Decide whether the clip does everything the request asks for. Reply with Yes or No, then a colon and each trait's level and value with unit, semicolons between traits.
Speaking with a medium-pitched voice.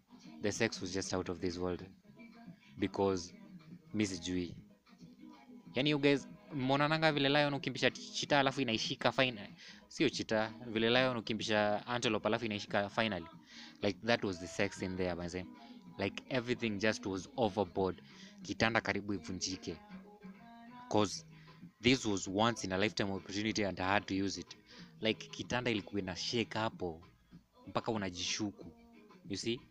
No: low, 110 Hz